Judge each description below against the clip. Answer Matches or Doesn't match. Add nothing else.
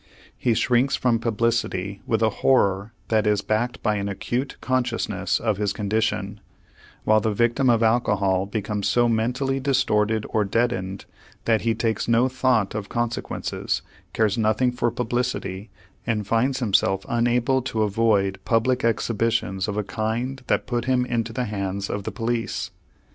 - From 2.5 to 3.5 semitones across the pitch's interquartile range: Matches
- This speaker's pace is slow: Doesn't match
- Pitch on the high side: Doesn't match